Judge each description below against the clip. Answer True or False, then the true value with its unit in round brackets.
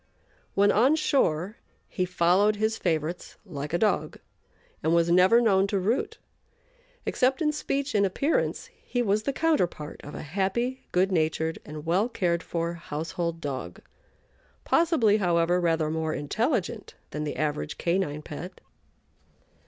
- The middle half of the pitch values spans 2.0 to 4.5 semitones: False (5.1 semitones)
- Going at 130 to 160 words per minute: True (140 wpm)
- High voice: False (180 Hz)